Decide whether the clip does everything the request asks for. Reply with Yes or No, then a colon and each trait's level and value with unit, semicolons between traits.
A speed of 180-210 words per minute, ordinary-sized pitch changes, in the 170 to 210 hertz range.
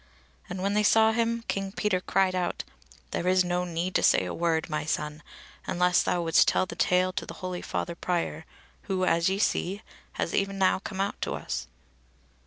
No: average, 195 wpm; narrow, 2.2 semitones; medium, 185 Hz